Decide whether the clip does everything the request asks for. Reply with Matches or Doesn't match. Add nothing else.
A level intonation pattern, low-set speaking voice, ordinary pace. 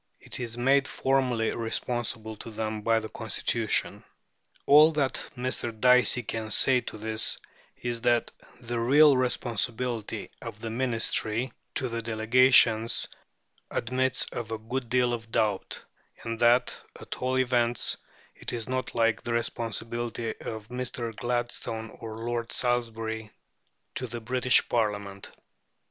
Doesn't match